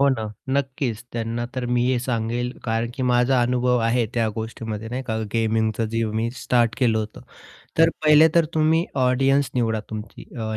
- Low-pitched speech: Yes, low, 120 Hz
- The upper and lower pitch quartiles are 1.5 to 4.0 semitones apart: Yes, narrow, 2.4 semitones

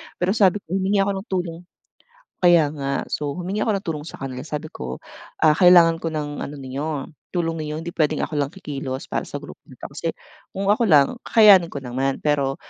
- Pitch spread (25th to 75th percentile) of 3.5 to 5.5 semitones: Yes, average, 4.7 semitones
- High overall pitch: No, medium, 160 Hz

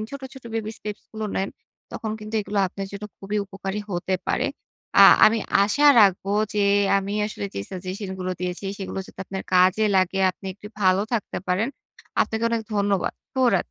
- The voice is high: Yes, high, 200 Hz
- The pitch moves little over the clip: Yes, narrow, 2.1 semitones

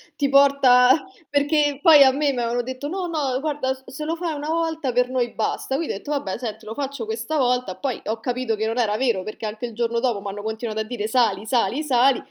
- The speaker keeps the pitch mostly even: No, average, 4.0 semitones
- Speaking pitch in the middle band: No, very high, 255 Hz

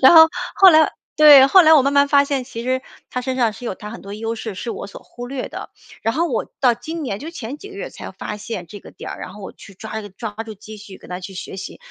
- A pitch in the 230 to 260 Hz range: Yes, high, 240 Hz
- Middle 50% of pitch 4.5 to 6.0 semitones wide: Yes, average, 5.1 semitones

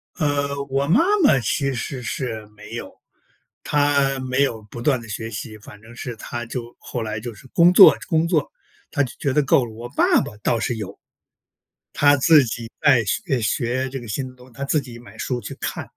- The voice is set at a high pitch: No, low, 125 Hz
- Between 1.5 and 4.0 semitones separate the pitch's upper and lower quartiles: Yes, average, 3.5 semitones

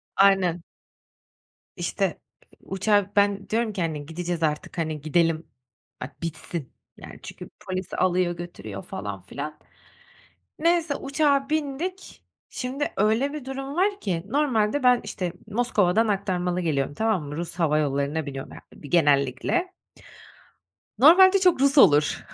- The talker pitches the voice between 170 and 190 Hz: Yes, medium, 185 Hz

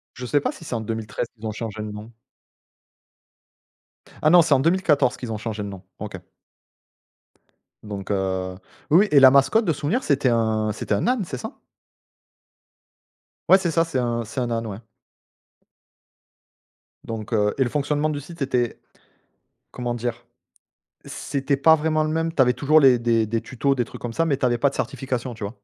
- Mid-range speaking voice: No, low, 125 Hz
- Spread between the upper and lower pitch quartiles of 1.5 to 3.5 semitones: No, average, 4.8 semitones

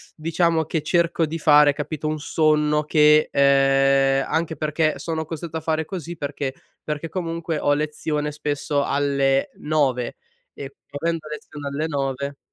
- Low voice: No, medium, 150 Hz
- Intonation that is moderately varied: No, narrow, 2.1 semitones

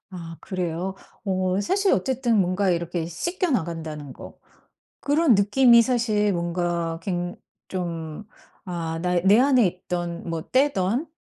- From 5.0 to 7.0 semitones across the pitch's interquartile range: Yes, wide, 5.4 semitones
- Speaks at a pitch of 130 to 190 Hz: Yes, medium, 185 Hz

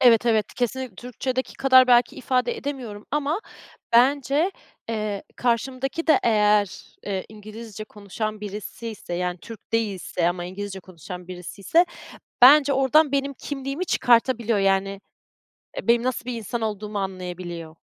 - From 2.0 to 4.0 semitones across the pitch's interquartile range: No, average, 4.6 semitones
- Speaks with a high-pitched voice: Yes, high, 225 Hz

